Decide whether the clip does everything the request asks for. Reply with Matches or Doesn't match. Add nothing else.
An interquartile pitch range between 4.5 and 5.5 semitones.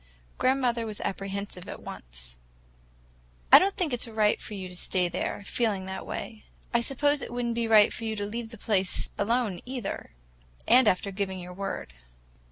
Doesn't match